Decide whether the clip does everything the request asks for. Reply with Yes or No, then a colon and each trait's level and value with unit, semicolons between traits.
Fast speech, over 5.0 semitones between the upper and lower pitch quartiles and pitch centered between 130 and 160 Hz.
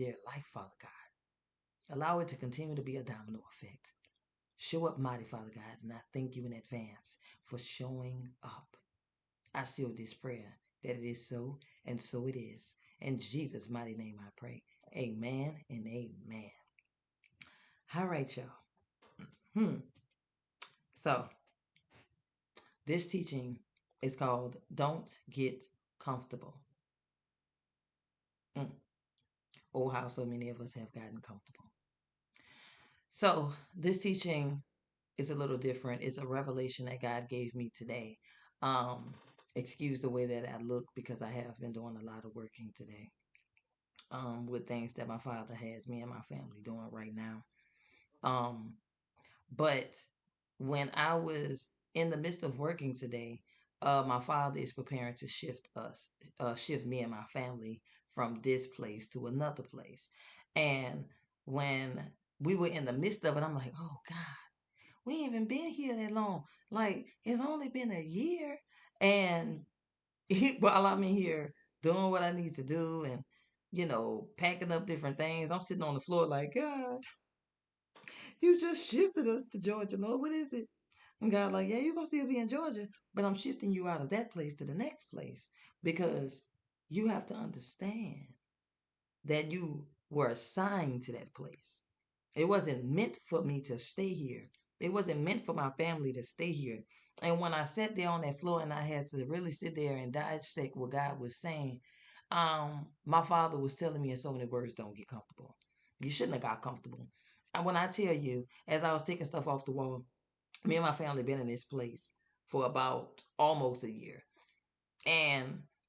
No: average, 170 wpm; wide, 5.6 semitones; medium, 140 Hz